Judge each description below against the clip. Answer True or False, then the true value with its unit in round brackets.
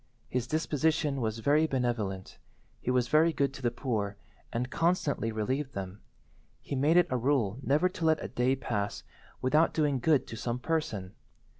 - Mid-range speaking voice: False (130 Hz)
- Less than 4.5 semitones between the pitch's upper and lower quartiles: False (4.9 semitones)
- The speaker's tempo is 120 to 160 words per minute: False (170 wpm)